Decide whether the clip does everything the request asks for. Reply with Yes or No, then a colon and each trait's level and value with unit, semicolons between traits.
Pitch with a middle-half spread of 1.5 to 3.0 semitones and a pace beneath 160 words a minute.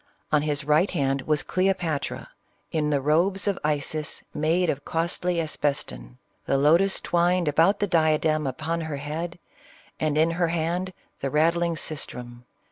Yes: average, 2.7 semitones; average, 145 wpm